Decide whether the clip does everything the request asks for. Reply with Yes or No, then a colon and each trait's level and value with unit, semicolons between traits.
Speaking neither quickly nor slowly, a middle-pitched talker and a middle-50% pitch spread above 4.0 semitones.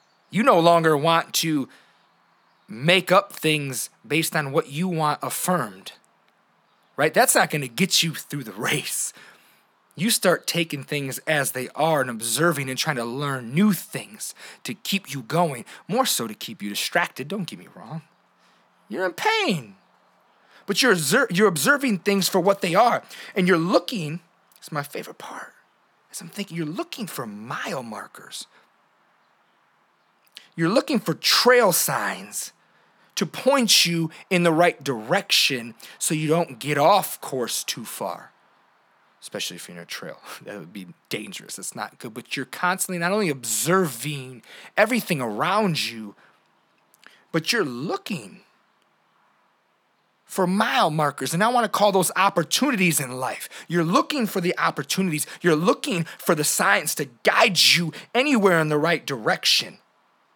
Yes: average, 155 wpm; medium, 170 Hz; average, 5.0 semitones